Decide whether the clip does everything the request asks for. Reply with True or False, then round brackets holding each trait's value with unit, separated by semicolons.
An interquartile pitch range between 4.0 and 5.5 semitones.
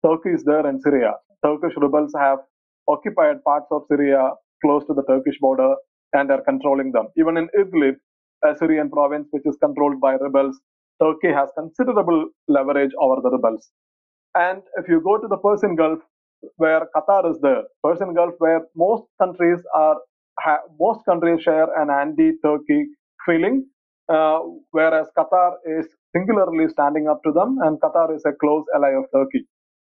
False (3.4 semitones)